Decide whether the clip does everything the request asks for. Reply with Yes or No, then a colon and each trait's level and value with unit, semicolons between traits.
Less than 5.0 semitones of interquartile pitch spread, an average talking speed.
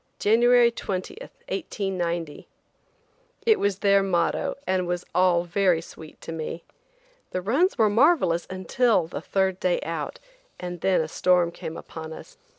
Yes: average, 3.6 semitones; average, 145 wpm